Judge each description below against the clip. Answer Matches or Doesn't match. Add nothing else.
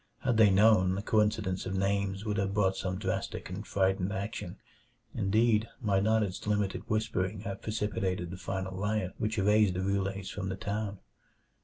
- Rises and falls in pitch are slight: Matches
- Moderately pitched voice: Doesn't match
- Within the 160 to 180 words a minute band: Matches